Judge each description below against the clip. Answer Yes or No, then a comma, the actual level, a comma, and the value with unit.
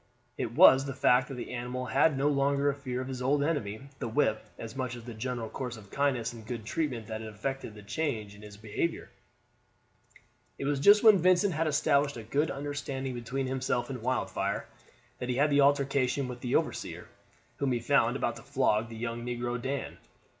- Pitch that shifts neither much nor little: Yes, average, 3.2 semitones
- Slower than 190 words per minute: No, fast, 205 wpm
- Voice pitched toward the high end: No, low, 130 Hz